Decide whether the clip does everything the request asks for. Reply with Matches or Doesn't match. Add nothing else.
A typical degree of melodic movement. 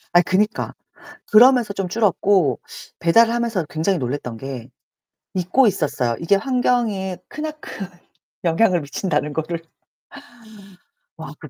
Doesn't match